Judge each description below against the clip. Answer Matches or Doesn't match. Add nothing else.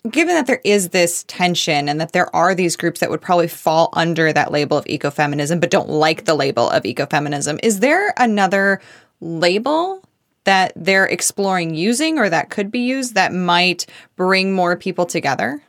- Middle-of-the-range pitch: Matches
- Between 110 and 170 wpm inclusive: Doesn't match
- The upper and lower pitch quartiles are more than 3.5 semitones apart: Matches